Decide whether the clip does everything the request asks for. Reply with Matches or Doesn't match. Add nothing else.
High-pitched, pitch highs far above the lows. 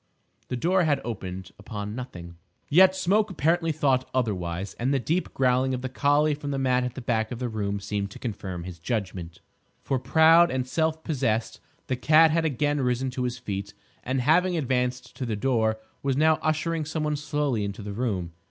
Doesn't match